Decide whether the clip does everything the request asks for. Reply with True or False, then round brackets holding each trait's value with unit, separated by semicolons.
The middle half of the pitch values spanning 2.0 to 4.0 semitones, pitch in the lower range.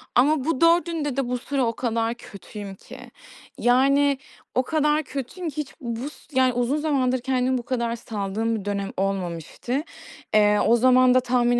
False (3.4 semitones; 250 Hz)